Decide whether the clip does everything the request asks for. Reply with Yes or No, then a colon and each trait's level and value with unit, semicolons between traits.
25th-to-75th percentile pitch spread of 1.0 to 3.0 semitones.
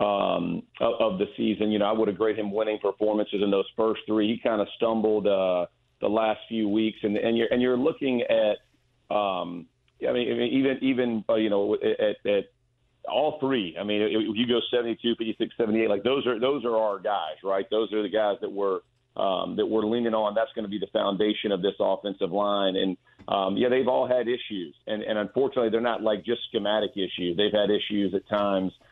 Yes: narrow, 2.6 semitones